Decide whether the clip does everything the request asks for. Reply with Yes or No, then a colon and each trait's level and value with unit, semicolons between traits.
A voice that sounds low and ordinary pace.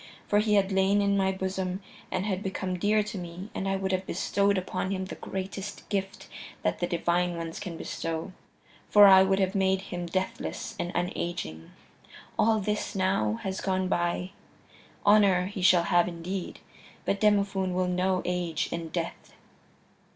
No: high, 190 Hz; average, 165 wpm